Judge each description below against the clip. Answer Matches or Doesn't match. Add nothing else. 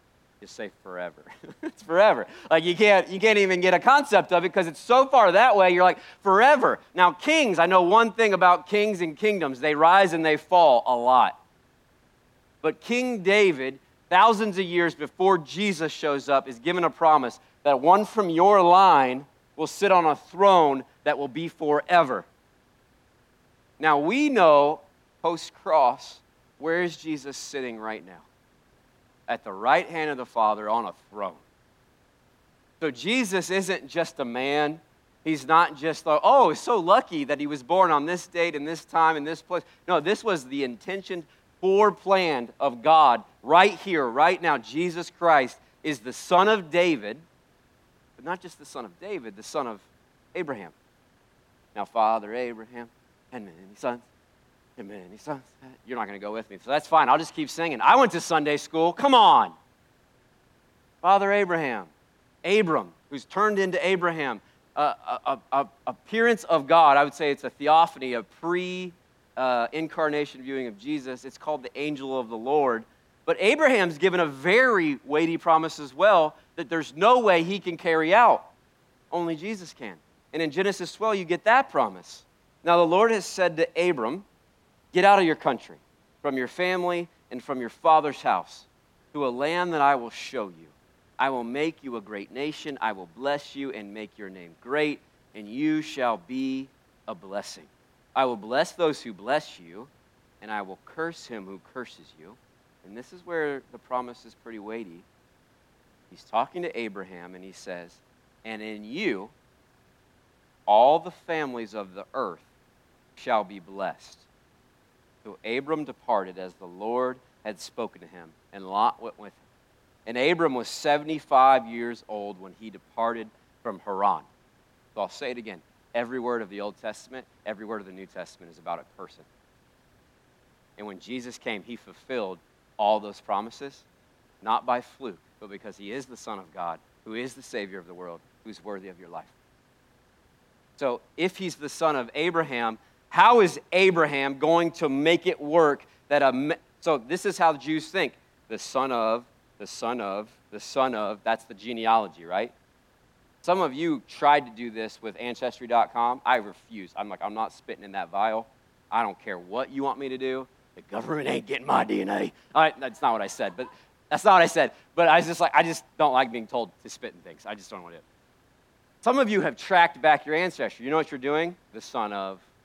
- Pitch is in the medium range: Matches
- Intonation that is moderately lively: Doesn't match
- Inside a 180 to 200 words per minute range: Matches